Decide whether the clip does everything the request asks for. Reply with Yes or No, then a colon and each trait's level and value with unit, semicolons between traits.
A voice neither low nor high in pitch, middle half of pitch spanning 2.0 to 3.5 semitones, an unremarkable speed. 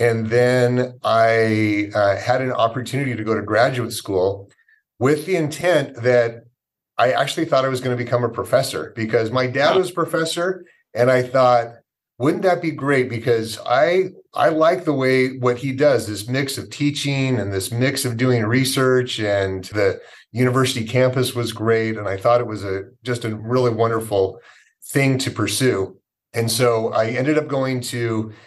No: low, 125 Hz; average, 2.8 semitones; average, 175 wpm